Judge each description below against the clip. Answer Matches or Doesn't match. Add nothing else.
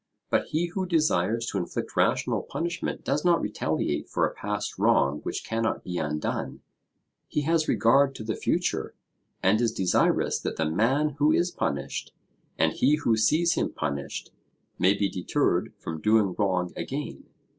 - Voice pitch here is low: Matches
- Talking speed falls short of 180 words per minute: Matches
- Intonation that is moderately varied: Doesn't match